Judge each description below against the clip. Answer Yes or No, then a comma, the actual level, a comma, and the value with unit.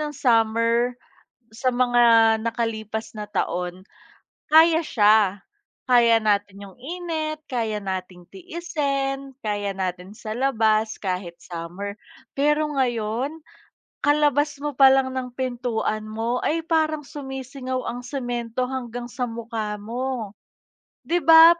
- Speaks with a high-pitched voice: Yes, high, 240 Hz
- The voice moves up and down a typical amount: Yes, average, 4.1 semitones